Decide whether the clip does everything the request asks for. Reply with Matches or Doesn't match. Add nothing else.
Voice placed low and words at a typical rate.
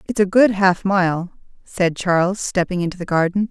Doesn't match